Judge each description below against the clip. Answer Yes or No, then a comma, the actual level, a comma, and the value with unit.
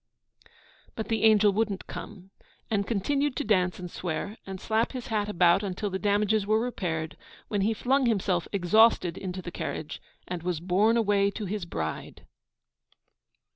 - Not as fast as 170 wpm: Yes, average, 160 wpm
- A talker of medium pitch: No, high, 200 Hz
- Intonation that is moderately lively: Yes, average, 3.3 semitones